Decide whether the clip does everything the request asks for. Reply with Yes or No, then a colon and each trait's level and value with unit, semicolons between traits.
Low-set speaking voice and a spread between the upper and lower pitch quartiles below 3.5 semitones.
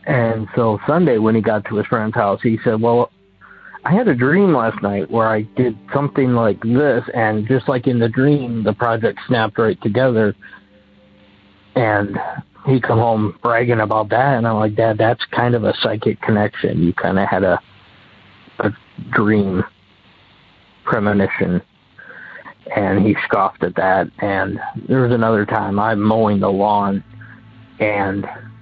Yes: low, 110 Hz; narrow, 2.4 semitones